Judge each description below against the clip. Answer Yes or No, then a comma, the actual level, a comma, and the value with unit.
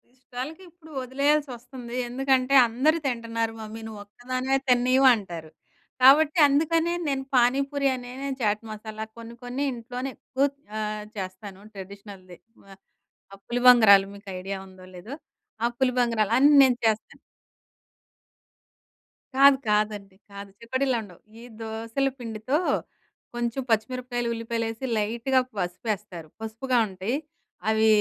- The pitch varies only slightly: No, average, 3.7 semitones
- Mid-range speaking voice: No, high, 235 Hz